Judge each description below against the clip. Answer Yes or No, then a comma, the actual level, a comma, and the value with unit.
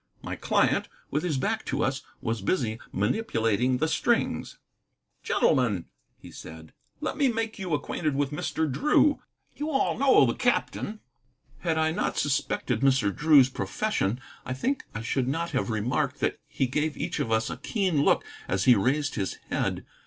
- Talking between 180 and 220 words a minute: No, average, 165 wpm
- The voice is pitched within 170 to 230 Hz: No, medium, 140 Hz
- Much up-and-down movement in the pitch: Yes, wide, 7.4 semitones